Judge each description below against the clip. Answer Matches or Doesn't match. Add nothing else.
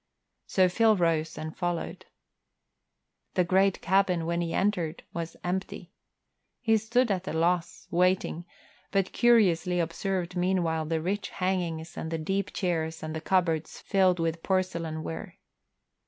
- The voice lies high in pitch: Doesn't match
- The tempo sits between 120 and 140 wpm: Matches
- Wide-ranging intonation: Doesn't match